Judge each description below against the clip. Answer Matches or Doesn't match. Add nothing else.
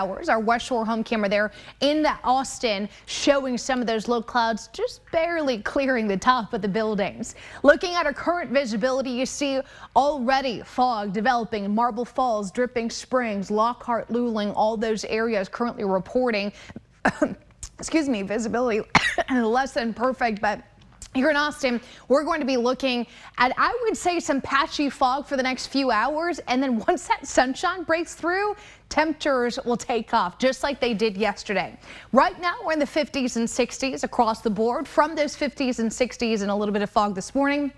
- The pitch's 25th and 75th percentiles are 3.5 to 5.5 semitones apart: Matches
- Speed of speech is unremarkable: Matches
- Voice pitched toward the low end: Doesn't match